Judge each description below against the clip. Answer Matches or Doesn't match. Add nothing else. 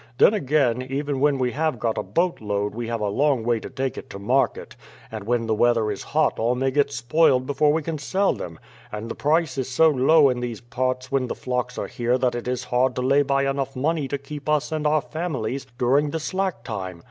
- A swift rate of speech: Matches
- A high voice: Doesn't match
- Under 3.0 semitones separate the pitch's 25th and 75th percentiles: Doesn't match